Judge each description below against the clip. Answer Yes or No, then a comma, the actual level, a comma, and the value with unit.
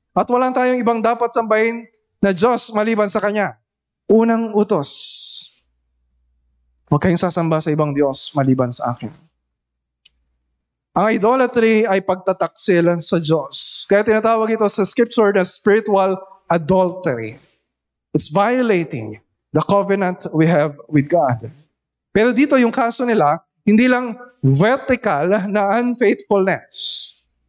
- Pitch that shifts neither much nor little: No, wide, 7.3 semitones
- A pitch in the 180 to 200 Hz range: Yes, high, 190 Hz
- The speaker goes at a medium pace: Yes, average, 120 wpm